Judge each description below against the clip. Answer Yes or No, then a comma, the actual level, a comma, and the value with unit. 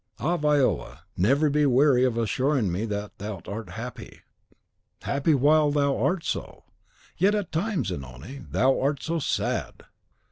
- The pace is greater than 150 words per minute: No, average, 145 wpm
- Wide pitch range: Yes, wide, 5.7 semitones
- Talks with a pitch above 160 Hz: No, low, 135 Hz